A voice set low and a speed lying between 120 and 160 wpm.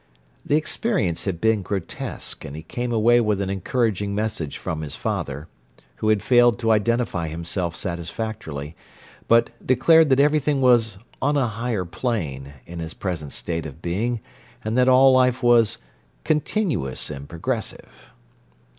Yes: low, 110 Hz; average, 145 wpm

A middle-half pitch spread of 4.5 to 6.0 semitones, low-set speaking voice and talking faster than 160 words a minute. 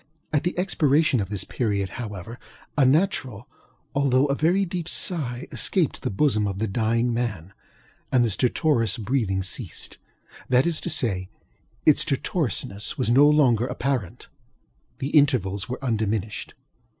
No: wide, 5.5 semitones; low, 125 Hz; average, 140 wpm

